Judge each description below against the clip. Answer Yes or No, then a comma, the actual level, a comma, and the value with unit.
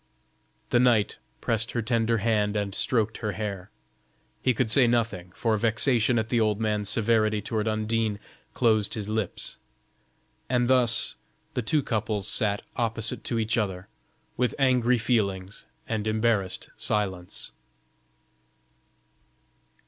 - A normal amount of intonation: No, narrow, 2.0 semitones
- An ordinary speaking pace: No, slow, 125 wpm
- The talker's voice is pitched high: No, low, 110 Hz